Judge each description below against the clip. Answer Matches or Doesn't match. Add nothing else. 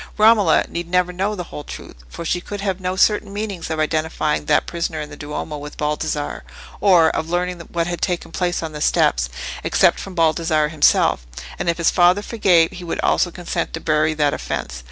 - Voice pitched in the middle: Matches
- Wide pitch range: Doesn't match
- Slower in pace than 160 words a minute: Doesn't match